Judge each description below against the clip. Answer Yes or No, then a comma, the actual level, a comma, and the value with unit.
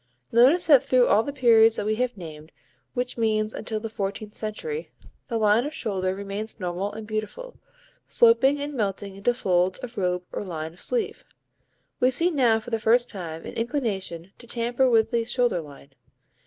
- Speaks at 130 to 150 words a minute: No, average, 180 wpm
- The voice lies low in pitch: No, high, 220 Hz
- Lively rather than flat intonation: No, average, 4.1 semitones